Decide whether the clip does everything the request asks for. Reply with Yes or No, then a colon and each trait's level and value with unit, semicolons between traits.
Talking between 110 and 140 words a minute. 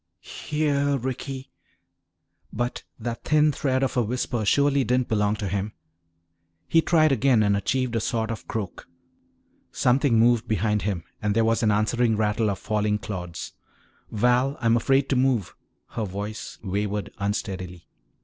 No: average, 150 wpm